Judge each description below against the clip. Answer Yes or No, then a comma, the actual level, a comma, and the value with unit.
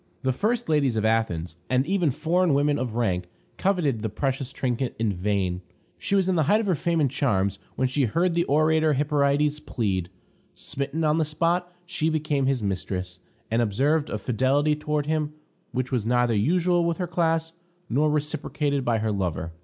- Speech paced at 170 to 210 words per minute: Yes, average, 185 wpm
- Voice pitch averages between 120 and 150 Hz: Yes, medium, 140 Hz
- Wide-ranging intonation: Yes, wide, 5.8 semitones